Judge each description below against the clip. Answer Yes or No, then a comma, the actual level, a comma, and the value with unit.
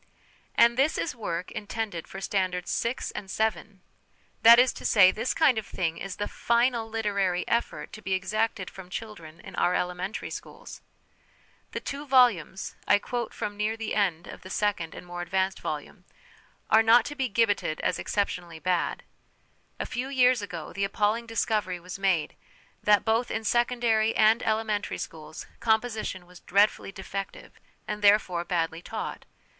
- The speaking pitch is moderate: No, high, 205 Hz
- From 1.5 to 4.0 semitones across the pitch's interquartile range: Yes, average, 3.7 semitones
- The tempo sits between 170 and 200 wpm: No, average, 160 wpm